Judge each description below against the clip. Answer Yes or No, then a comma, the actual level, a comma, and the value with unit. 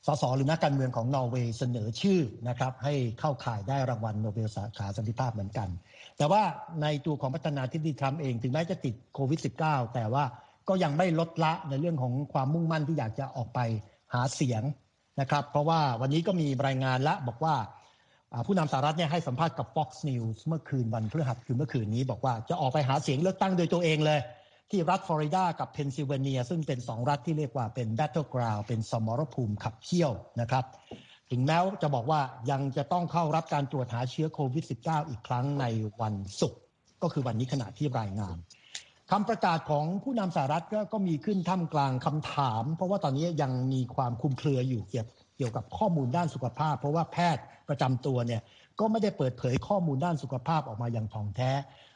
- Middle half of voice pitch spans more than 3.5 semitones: Yes, average, 4.3 semitones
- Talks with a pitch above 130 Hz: Yes, medium, 140 Hz